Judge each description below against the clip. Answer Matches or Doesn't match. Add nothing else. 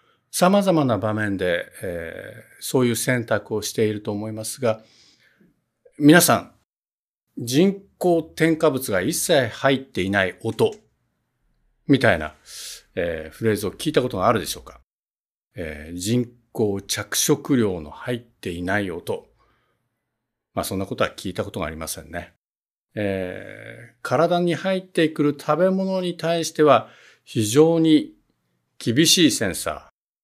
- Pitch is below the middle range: Matches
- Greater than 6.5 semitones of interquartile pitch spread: Matches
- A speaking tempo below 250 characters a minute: Doesn't match